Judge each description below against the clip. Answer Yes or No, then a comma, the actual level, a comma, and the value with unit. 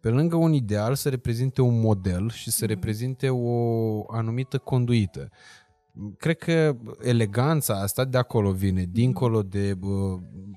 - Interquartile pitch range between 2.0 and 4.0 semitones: Yes, average, 3.7 semitones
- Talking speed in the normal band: Yes, average, 135 wpm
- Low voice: Yes, low, 115 Hz